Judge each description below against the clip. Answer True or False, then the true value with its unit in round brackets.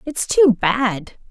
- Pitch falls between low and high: False (235 Hz)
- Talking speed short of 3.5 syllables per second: True (2.8 syllables/s)